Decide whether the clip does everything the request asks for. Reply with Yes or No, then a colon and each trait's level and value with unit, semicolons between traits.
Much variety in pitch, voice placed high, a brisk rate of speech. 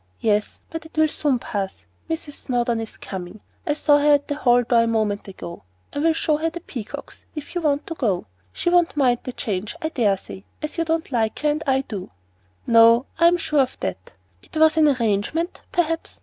Yes: wide, 6.0 semitones; very high, 270 Hz; fast, 215 wpm